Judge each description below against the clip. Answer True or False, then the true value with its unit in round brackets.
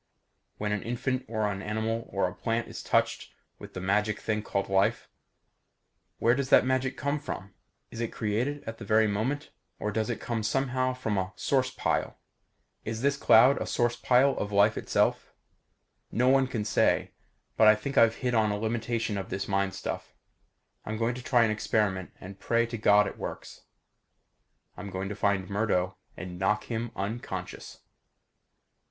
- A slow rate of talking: False (175 wpm)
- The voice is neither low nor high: False (110 Hz)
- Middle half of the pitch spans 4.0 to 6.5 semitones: False (3.0 semitones)